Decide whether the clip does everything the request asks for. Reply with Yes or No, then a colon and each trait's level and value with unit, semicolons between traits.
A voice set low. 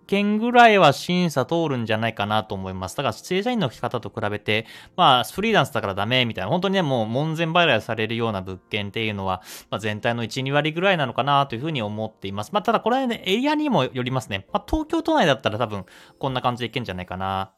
Yes: low, 125 Hz